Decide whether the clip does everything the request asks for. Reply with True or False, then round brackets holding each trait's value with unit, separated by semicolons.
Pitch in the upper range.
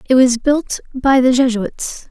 True (255 Hz)